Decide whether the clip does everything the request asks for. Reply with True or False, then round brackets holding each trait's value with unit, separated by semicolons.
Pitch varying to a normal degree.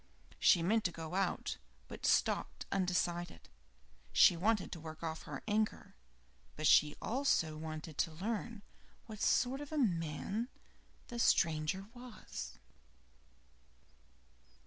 False (5.7 semitones)